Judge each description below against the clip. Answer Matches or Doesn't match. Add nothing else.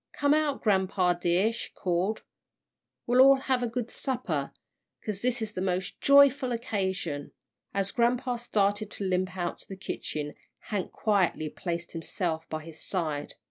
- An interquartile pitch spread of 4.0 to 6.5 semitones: Matches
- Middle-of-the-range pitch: Doesn't match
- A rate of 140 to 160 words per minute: Matches